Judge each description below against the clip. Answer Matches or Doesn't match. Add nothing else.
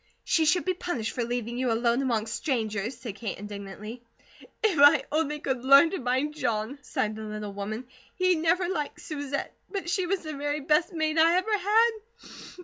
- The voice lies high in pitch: Matches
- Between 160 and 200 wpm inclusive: Matches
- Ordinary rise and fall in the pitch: Doesn't match